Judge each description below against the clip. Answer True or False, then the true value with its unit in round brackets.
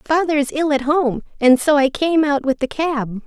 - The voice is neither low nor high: False (285 Hz)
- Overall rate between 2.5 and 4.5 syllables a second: True (4.3 syllables/s)